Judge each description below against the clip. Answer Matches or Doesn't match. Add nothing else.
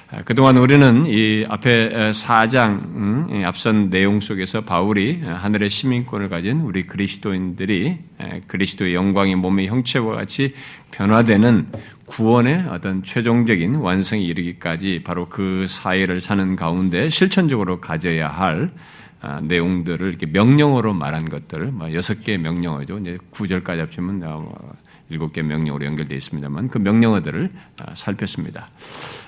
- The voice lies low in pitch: Matches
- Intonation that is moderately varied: Matches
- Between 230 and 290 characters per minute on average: Doesn't match